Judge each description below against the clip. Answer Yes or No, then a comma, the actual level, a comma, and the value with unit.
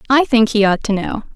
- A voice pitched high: Yes, high, 230 Hz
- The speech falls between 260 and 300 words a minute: Yes, fast, 265 wpm